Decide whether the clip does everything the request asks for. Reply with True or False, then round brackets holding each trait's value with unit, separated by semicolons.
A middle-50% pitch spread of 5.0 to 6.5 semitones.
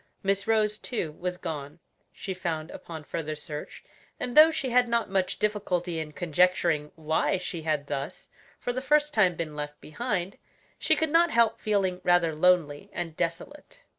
True (5.6 semitones)